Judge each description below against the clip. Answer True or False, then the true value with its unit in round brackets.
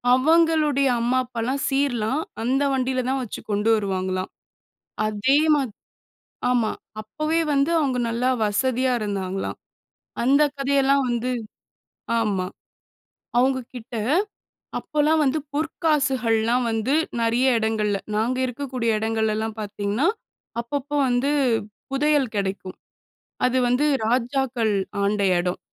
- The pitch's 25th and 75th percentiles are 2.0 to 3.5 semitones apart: False (4.0 semitones)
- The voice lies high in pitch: True (250 Hz)